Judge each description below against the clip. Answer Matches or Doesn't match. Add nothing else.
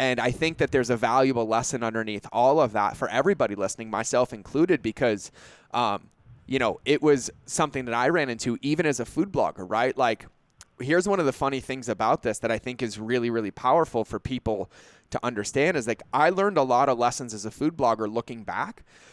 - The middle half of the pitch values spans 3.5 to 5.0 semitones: Doesn't match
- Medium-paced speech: Doesn't match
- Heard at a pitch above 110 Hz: Matches